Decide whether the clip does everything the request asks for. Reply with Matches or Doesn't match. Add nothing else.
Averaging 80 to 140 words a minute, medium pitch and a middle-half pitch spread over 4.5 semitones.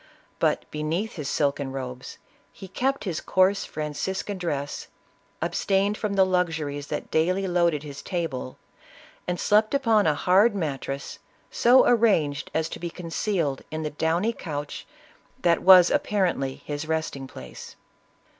Matches